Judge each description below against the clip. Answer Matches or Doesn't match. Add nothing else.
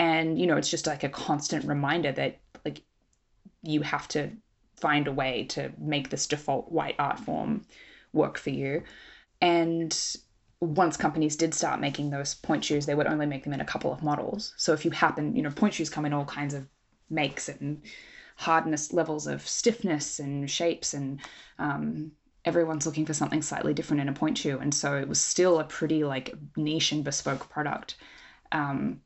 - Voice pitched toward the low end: Doesn't match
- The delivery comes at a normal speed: Matches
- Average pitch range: Doesn't match